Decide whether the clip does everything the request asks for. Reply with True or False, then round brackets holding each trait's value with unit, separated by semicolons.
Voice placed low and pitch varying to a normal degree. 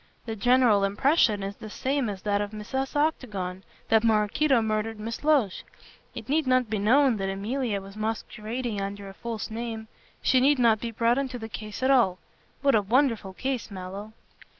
False (225 Hz; 3.9 semitones)